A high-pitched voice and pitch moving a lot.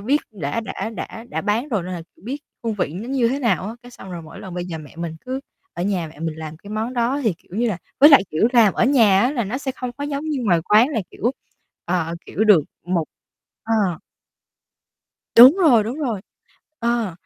Yes: high, 220 Hz; wide, 5.9 semitones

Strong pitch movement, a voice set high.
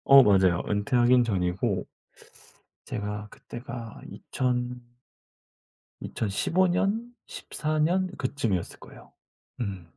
No: wide, 5.8 semitones; low, 120 Hz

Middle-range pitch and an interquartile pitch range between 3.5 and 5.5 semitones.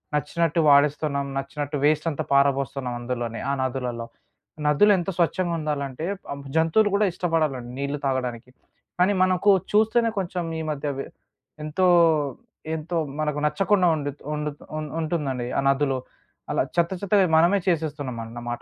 Yes: medium, 150 Hz; average, 4.0 semitones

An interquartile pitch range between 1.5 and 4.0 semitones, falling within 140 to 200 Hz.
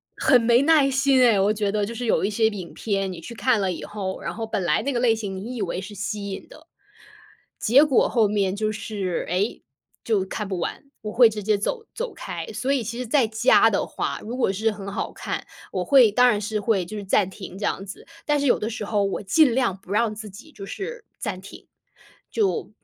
No: average, 3.6 semitones; high, 215 Hz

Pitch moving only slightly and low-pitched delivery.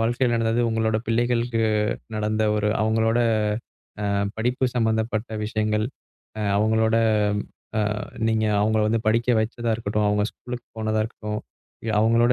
Yes: narrow, 1.3 semitones; low, 110 Hz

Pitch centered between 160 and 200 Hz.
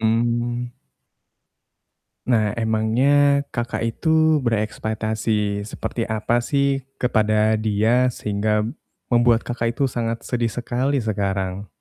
No: low, 115 Hz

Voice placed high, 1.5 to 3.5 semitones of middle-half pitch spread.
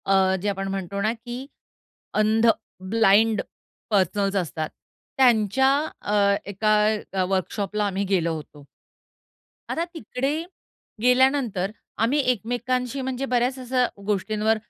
No: high, 215 Hz; average, 4.1 semitones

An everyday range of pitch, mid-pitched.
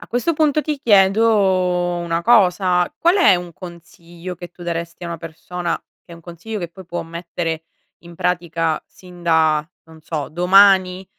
No: narrow, 2.2 semitones; medium, 175 Hz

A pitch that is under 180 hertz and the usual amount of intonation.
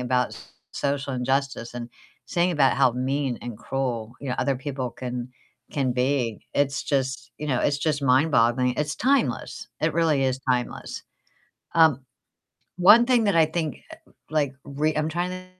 Yes: low, 135 Hz; average, 3.4 semitones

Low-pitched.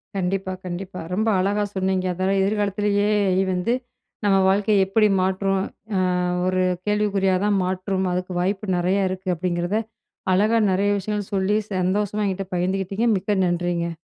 No: high, 195 Hz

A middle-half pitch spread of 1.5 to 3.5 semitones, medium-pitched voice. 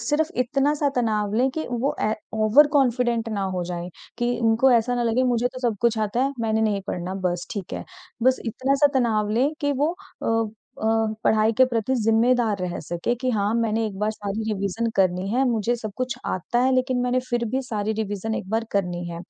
No: average, 2.9 semitones; high, 225 Hz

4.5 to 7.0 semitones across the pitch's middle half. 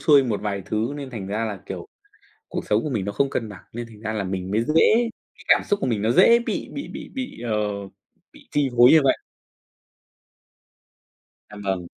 Yes: average, 5.1 semitones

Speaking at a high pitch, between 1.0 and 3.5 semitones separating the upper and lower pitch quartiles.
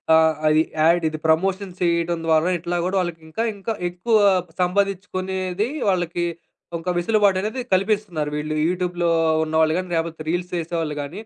No: medium, 175 Hz; average, 2.7 semitones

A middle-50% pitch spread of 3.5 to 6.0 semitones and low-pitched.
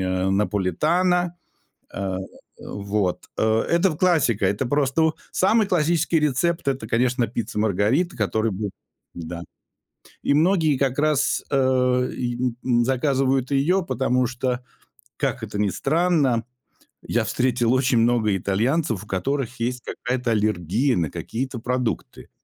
Yes: average, 5.0 semitones; low, 125 Hz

